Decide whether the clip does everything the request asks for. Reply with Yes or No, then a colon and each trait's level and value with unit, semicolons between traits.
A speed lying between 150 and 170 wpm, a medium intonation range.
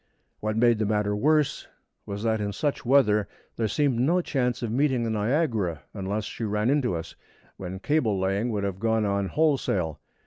No: average, 180 wpm; average, 4.2 semitones